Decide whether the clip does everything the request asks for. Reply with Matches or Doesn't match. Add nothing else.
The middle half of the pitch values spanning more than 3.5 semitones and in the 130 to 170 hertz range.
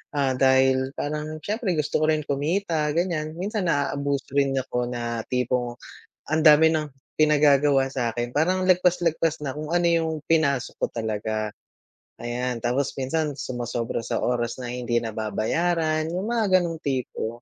Matches